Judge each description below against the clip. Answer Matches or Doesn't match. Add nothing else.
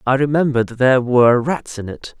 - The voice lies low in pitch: Matches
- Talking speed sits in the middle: Matches